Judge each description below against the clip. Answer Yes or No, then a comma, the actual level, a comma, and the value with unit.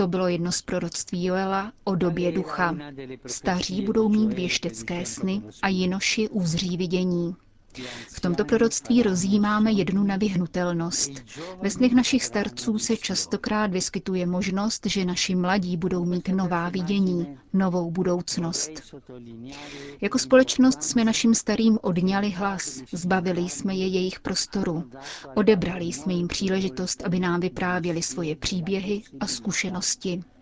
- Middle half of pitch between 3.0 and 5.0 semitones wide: No, narrow, 2.5 semitones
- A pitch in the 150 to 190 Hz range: Yes, medium, 185 Hz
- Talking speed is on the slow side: No, average, 125 wpm